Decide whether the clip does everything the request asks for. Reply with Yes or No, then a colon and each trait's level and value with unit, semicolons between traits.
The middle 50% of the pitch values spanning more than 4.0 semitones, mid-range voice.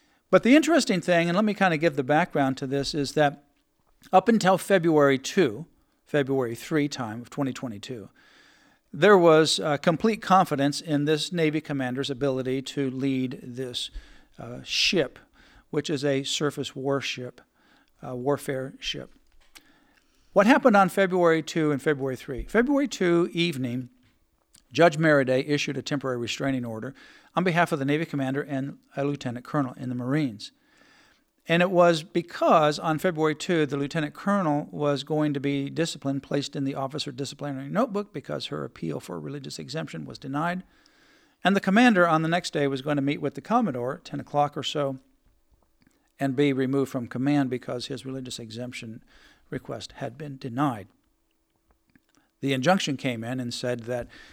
Yes: average, 4.4 semitones; medium, 145 Hz